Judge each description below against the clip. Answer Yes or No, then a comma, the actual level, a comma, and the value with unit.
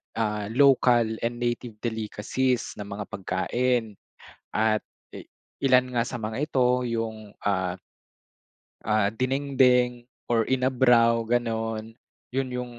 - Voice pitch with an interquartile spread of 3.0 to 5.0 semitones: No, narrow, 2.4 semitones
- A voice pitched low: Yes, low, 120 Hz